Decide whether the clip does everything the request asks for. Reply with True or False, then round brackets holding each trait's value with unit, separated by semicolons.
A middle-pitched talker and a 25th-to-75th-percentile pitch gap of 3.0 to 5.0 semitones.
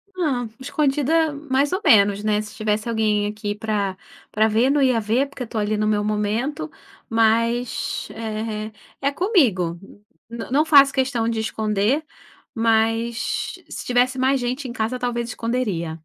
False (230 Hz; 3.6 semitones)